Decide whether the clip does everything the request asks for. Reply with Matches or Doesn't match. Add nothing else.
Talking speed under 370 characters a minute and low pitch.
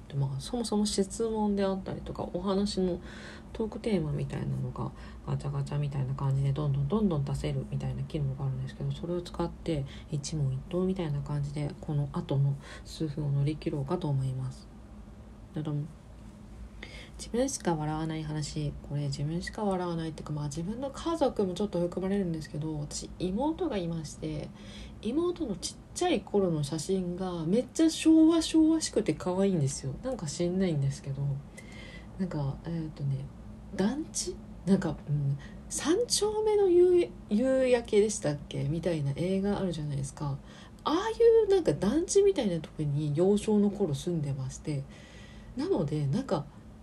Doesn't match